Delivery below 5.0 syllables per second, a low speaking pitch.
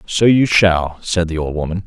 Yes: 4.7 syllables/s; very low, 90 Hz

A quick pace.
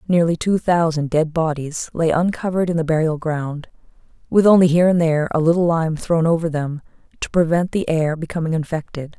No: average, 185 wpm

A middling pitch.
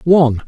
Yes: medium, 145 Hz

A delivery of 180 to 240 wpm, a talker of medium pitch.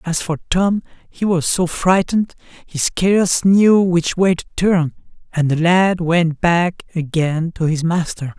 No: average, 165 wpm; medium, 170 Hz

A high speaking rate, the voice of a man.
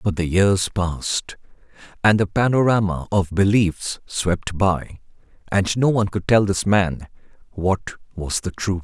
No: average, 150 wpm; male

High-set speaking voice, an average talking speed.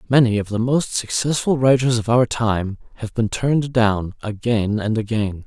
No: low, 115 Hz; average, 175 wpm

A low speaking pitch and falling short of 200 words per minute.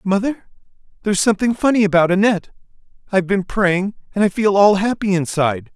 No: high, 195 Hz; average, 155 wpm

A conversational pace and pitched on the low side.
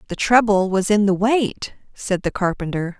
No: average, 180 wpm; high, 200 Hz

